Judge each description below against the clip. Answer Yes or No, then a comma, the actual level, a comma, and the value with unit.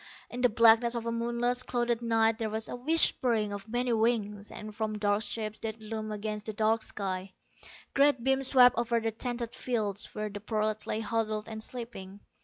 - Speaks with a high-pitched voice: Yes, high, 225 Hz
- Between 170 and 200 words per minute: Yes, average, 190 wpm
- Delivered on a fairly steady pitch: Yes, narrow, 2.0 semitones